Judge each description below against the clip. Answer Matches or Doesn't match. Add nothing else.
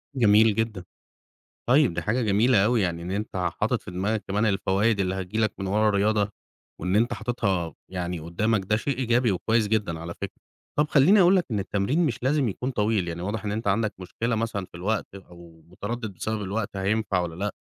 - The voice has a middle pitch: Doesn't match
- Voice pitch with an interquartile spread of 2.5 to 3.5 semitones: Matches